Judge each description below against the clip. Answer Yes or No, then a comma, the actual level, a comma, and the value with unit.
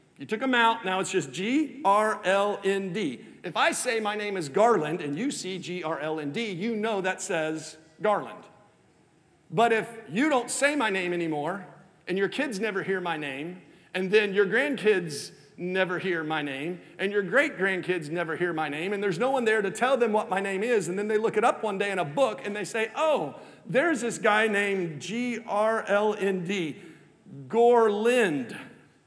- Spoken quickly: No, average, 180 wpm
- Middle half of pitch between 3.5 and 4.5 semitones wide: Yes, average, 4.0 semitones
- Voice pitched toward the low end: No, high, 200 Hz